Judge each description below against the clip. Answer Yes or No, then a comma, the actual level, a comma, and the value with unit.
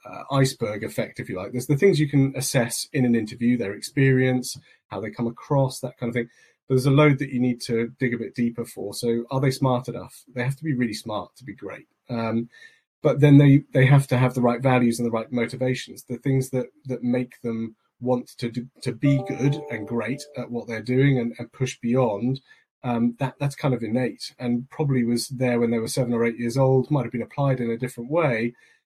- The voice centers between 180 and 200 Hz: No, low, 125 Hz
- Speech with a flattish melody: Yes, narrow, 2.2 semitones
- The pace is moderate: No, fast, 235 wpm